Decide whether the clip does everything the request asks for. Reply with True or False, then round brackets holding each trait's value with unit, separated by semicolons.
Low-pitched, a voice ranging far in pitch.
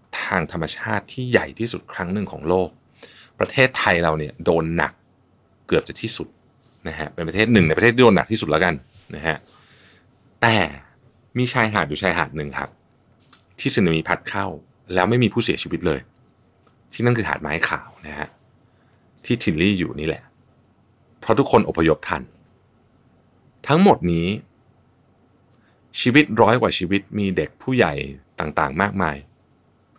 True (100 Hz; 6.2 semitones)